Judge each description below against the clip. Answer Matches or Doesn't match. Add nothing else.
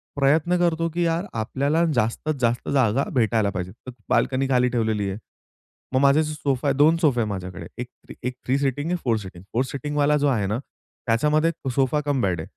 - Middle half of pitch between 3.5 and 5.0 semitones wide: Matches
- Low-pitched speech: Matches